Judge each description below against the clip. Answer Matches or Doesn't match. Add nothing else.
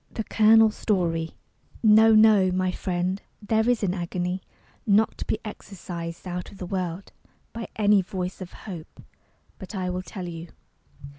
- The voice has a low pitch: Doesn't match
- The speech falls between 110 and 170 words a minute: Matches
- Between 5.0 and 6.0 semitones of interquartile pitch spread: Doesn't match